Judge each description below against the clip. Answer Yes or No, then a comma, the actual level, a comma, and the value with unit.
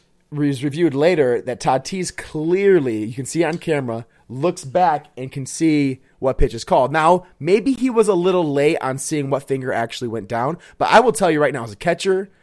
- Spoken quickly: Yes, fast, 215 wpm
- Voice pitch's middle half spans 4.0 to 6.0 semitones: Yes, average, 5.2 semitones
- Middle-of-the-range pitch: Yes, medium, 150 Hz